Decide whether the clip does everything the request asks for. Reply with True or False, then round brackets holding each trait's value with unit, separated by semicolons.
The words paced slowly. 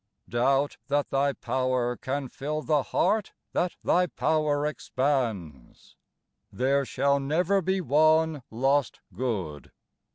True (110 wpm)